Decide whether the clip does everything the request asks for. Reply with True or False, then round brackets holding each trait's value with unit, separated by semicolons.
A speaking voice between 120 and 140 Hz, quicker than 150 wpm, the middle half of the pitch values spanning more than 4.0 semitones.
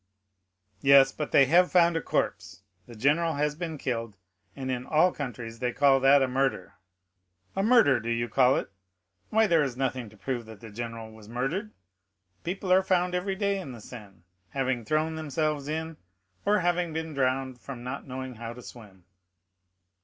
True (135 Hz; 180 wpm; 5.2 semitones)